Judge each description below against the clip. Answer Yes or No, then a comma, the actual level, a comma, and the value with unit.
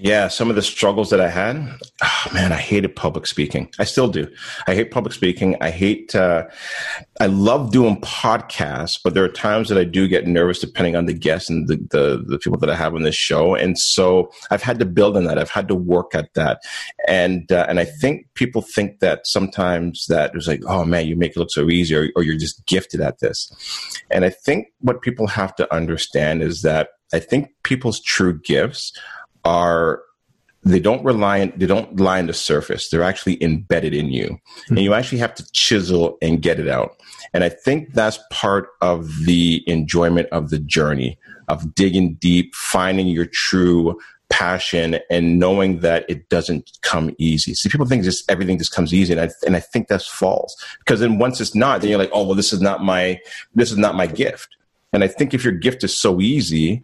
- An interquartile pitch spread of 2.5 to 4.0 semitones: Yes, average, 3.3 semitones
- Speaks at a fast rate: Yes, fast, 215 wpm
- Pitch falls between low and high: No, very low, 90 Hz